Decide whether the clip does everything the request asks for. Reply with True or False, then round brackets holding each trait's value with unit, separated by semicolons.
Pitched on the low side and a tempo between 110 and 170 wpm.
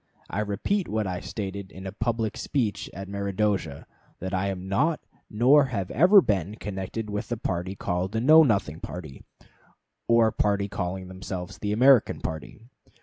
True (100 Hz; 160 wpm)